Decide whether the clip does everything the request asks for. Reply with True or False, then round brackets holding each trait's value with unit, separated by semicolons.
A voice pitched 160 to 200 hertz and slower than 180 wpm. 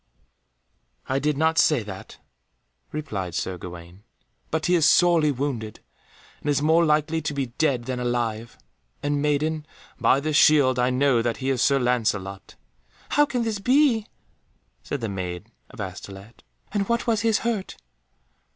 False (140 Hz; 155 wpm)